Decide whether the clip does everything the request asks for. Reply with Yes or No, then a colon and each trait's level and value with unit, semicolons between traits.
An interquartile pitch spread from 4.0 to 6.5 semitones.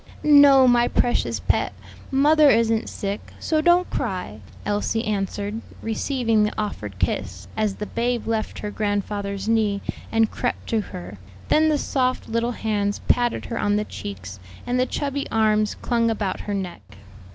No: average, 3.2 semitones